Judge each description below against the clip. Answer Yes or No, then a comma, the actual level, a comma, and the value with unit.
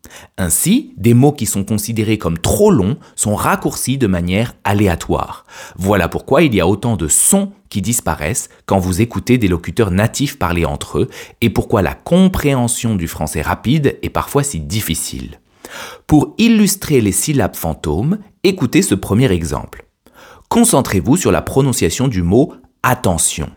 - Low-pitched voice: Yes, low, 105 Hz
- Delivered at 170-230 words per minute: No, average, 155 wpm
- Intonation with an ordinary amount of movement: No, wide, 6.8 semitones